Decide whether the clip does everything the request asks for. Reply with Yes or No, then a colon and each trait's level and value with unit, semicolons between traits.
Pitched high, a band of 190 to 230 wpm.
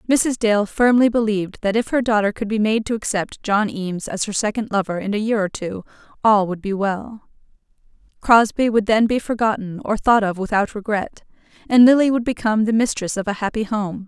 Yes: high, 215 Hz; fast, 205 wpm